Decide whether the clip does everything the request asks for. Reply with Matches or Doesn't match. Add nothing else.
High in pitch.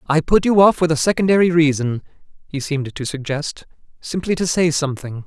Doesn't match